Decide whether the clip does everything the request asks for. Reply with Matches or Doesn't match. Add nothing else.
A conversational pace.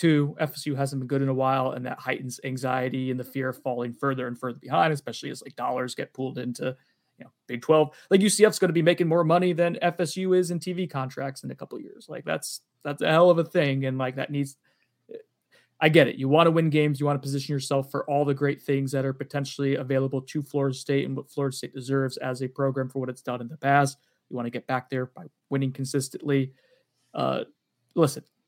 Doesn't match